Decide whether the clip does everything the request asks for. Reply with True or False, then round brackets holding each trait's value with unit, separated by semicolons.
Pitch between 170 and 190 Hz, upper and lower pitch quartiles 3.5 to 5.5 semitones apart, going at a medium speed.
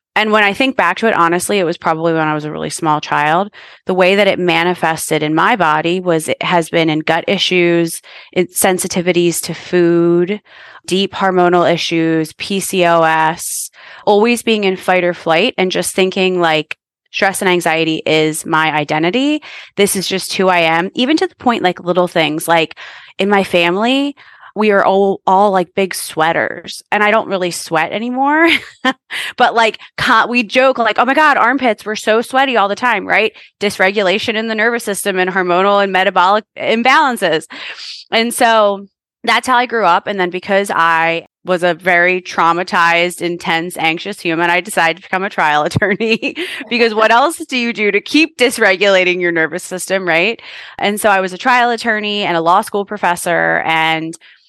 True (185 Hz; 4.1 semitones; 180 wpm)